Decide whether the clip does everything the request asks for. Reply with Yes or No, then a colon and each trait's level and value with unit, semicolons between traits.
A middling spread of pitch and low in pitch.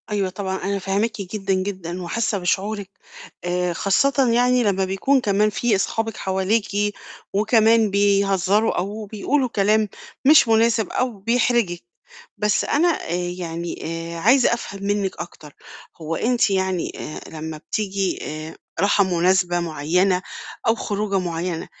No: average, 3.2 semitones; high, 200 Hz